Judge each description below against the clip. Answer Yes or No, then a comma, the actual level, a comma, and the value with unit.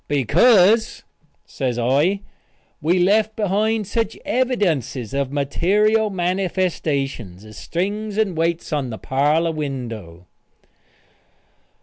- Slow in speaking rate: Yes, slow, 95 wpm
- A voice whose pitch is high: No, medium, 170 Hz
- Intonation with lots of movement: Yes, wide, 7.2 semitones